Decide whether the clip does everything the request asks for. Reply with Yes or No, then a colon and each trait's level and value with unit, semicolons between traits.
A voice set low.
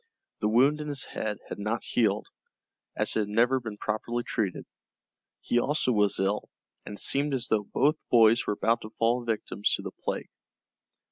Yes: low, 115 Hz